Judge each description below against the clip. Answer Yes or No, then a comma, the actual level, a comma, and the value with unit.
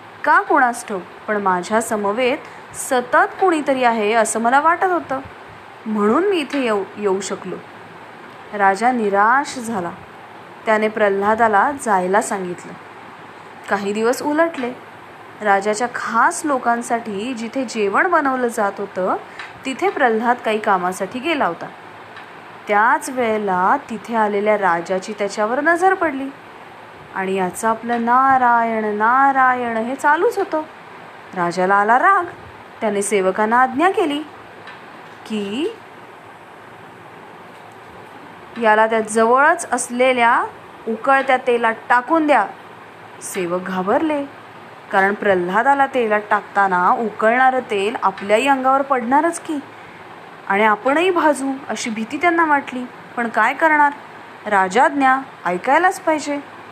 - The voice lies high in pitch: Yes, high, 235 Hz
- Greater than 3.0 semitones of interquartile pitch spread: Yes, average, 5.0 semitones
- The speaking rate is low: Yes, slow, 105 wpm